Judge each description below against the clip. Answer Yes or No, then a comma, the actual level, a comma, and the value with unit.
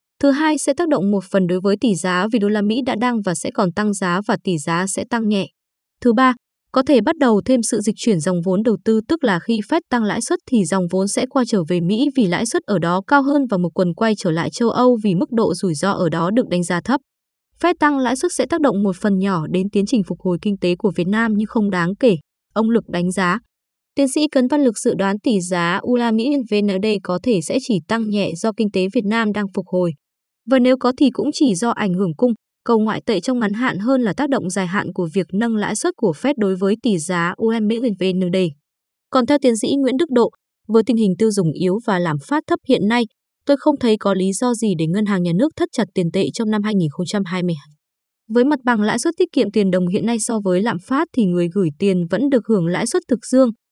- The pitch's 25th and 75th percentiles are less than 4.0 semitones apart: No, average, 4.9 semitones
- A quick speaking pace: Yes, fast, 265 wpm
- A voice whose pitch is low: No, high, 215 Hz